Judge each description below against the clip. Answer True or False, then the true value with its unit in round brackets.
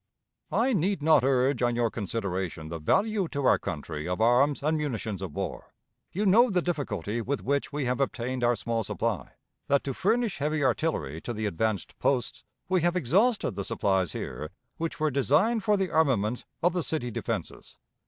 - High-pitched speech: False (135 Hz)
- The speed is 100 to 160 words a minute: False (185 wpm)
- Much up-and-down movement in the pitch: True (6.9 semitones)